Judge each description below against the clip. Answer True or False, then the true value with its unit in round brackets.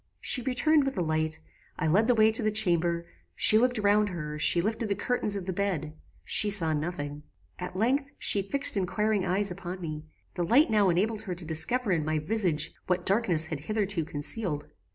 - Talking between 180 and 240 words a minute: True (195 wpm)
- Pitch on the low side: False (185 Hz)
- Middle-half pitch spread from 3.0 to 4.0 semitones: False (5.1 semitones)